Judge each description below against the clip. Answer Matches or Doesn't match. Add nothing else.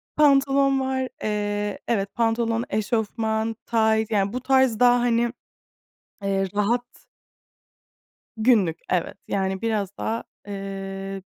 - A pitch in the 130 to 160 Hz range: Doesn't match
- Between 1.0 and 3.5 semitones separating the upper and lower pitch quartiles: Matches